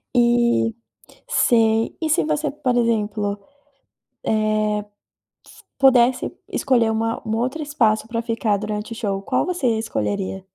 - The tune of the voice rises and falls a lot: No, narrow, 2.6 semitones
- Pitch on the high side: Yes, high, 225 Hz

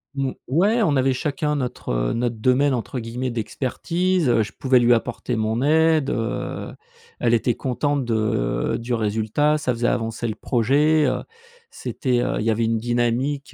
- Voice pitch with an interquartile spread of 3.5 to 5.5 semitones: Yes, average, 4.0 semitones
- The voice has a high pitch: No, low, 125 Hz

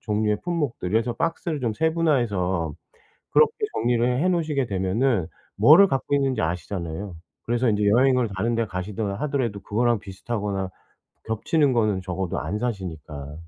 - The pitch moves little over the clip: No, wide, 5.5 semitones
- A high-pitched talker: No, low, 110 Hz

